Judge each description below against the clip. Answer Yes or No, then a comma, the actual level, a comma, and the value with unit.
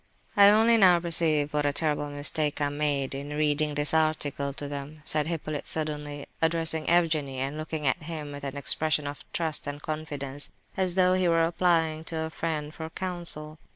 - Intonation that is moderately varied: No, narrow, 2.1 semitones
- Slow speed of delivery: No, average, 185 wpm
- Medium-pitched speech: Yes, medium, 155 Hz